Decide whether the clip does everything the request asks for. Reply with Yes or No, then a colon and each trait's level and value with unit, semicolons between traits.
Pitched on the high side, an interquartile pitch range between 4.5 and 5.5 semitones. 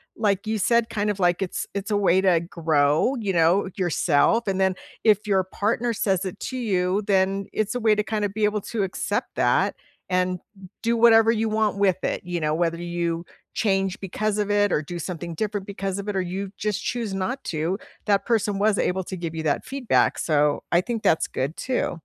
No: high, 195 Hz; average, 3.3 semitones